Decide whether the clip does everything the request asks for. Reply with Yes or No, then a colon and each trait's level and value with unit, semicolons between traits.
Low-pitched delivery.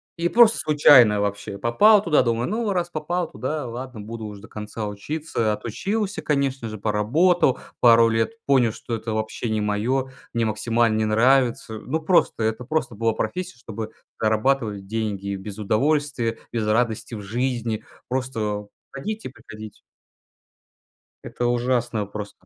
Yes: low, 115 Hz